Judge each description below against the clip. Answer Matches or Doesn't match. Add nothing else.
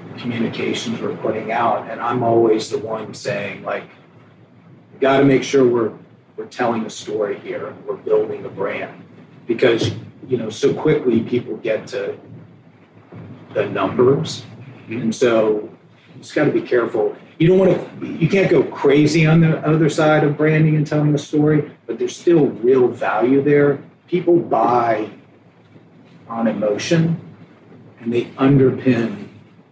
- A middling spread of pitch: Doesn't match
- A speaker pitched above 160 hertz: Doesn't match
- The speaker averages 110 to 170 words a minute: Matches